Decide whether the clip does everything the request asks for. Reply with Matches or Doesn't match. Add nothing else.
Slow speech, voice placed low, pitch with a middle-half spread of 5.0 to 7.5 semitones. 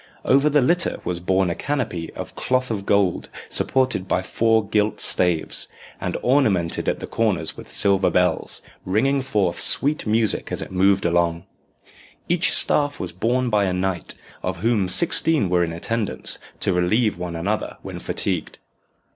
Doesn't match